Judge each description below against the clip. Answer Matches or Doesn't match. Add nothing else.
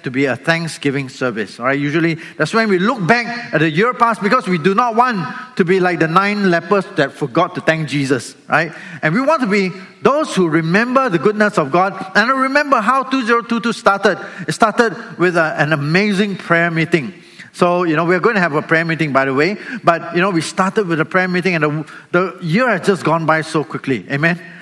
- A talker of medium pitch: Matches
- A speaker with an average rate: Doesn't match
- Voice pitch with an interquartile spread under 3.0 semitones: Doesn't match